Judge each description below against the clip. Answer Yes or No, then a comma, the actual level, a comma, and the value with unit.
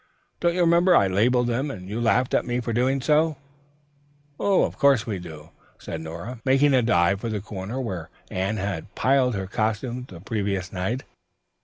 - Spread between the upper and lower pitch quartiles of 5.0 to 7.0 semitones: Yes, wide, 5.4 semitones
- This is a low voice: Yes, low, 115 Hz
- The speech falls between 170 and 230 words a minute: Yes, average, 180 wpm